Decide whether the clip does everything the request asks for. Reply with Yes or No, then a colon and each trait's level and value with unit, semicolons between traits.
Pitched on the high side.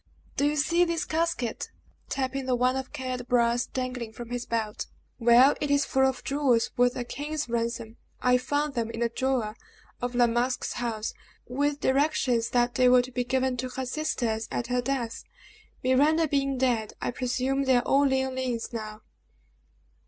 Yes: very high, 255 Hz